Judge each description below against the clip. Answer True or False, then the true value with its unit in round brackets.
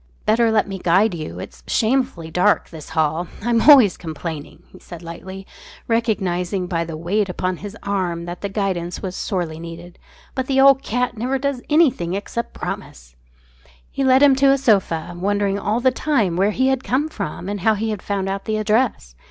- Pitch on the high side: True (200 Hz)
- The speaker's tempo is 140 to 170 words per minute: False (190 wpm)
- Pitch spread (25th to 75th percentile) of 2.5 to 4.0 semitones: False (5.3 semitones)